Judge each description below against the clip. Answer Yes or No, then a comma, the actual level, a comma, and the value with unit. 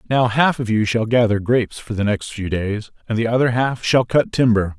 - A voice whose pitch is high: No, low, 115 Hz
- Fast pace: Yes, fast, 240 wpm